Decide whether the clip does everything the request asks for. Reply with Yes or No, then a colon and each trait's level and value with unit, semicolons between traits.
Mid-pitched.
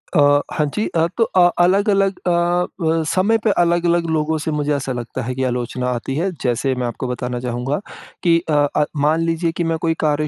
Yes: medium, 155 Hz